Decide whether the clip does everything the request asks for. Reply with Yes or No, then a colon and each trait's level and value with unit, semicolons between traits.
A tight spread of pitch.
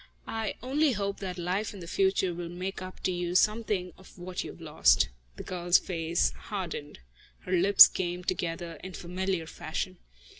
Yes: narrow, 1.9 semitones